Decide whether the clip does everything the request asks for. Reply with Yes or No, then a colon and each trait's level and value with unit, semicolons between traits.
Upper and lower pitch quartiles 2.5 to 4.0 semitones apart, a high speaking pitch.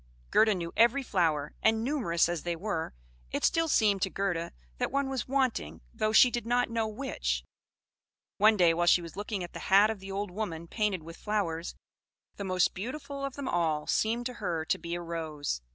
No: wide, 5.4 semitones; high, 200 Hz